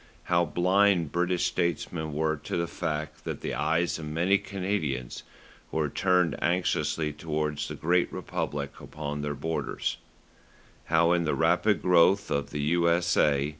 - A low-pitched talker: Yes, very low, 80 Hz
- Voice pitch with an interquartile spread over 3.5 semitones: No, average, 2.7 semitones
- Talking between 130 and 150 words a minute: Yes, average, 140 wpm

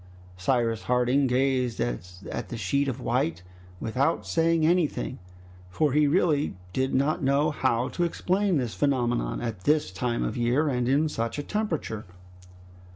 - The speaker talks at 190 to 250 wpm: No, average, 150 wpm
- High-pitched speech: No, low, 130 Hz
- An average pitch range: Yes, average, 4.5 semitones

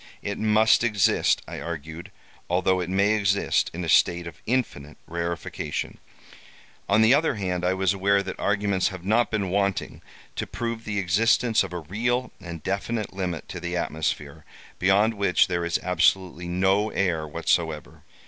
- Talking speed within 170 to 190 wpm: No, average, 160 wpm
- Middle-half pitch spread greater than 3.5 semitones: No, average, 3.2 semitones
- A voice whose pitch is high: No, very low, 95 Hz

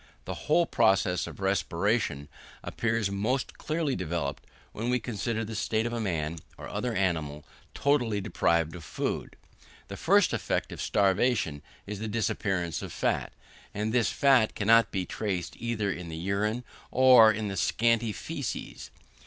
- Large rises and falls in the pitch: No, average, 4.3 semitones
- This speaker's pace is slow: No, average, 155 wpm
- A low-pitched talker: Yes, low, 105 Hz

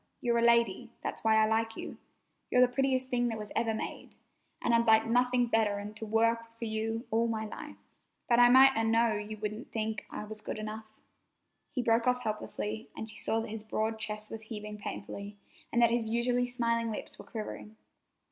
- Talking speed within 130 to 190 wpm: No, fast, 205 wpm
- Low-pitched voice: No, high, 225 Hz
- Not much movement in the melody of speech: Yes, narrow, 1.5 semitones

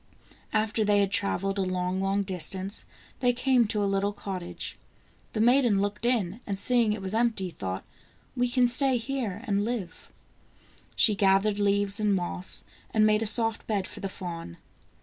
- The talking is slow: No, average, 170 wpm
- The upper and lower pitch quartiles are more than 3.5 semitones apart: No, average, 2.8 semitones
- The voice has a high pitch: Yes, high, 205 Hz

